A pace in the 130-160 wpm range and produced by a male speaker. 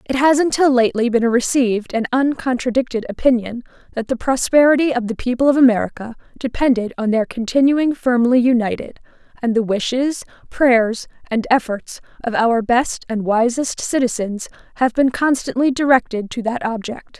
No: average, 150 wpm; female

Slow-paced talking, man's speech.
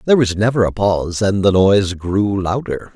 No: fast, 205 wpm; male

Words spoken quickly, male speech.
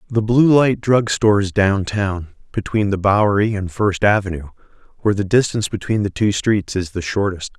No: average, 180 wpm; male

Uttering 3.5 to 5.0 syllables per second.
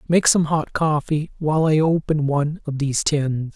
Yes: 4.9 syllables/s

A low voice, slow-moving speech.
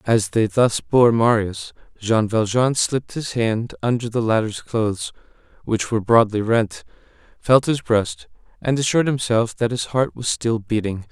No: low, 115 Hz; average, 160 wpm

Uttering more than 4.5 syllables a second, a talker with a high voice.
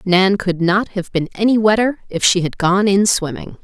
Yes: 4.7 syllables/s; high, 195 Hz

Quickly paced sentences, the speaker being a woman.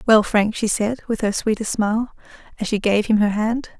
Yes: fast, 220 wpm; female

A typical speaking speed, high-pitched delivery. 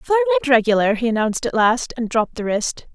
No: fast, 225 wpm; very high, 250 Hz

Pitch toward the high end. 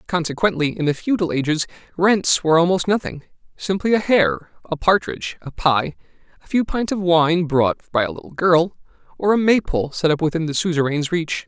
No: medium, 170 Hz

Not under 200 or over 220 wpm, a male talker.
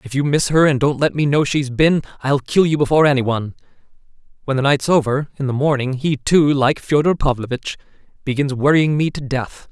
Yes: fast, 205 wpm; male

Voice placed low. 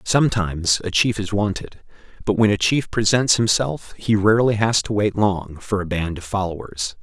Yes: low, 105 Hz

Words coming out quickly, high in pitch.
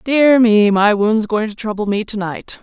Yes: fast, 230 wpm; high, 215 Hz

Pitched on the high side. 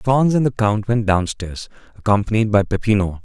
No: low, 105 Hz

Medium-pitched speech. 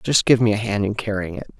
No: low, 105 Hz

